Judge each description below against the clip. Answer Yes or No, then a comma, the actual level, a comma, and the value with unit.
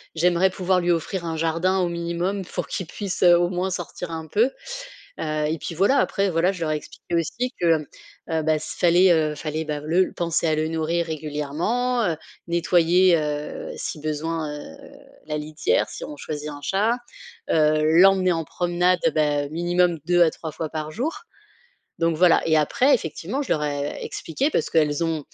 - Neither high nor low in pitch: Yes, medium, 165 Hz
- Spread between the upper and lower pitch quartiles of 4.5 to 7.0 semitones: No, average, 2.7 semitones